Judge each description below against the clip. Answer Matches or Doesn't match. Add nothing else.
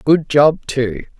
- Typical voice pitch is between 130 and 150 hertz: Matches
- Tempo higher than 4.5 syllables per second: Doesn't match